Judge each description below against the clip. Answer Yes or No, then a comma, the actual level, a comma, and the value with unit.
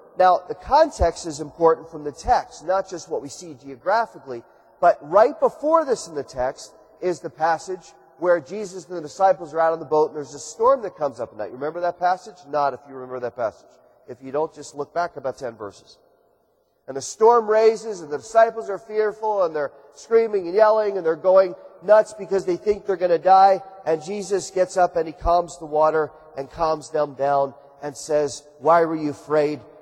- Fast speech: Yes, fast, 210 wpm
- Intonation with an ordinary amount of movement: Yes, average, 4.7 semitones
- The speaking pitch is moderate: Yes, medium, 165 Hz